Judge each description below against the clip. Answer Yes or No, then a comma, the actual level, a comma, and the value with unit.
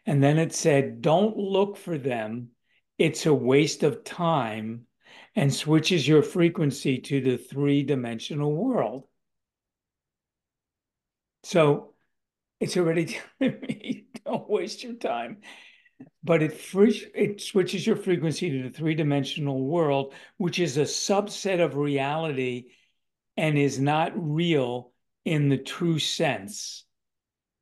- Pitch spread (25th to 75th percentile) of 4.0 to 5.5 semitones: Yes, average, 5.2 semitones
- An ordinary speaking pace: No, slow, 125 wpm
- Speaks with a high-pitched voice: No, medium, 155 Hz